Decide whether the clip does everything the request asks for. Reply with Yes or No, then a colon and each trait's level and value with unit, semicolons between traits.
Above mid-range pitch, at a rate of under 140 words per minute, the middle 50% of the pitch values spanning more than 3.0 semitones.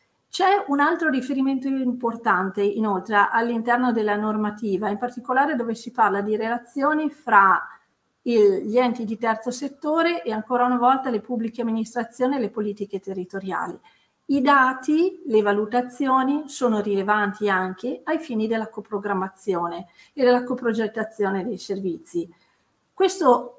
Yes: high, 235 Hz; average, 130 wpm; average, 4.1 semitones